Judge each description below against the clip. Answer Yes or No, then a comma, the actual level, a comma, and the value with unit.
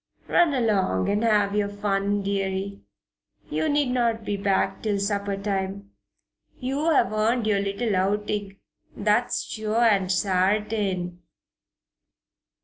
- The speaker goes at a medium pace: No, slow, 120 wpm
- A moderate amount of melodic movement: No, narrow, 1.9 semitones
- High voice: Yes, high, 205 Hz